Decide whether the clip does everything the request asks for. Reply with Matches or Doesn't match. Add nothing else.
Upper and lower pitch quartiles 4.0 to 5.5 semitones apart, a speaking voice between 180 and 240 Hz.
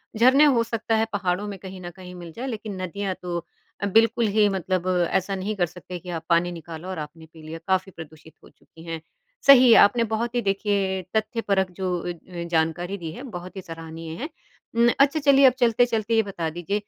Matches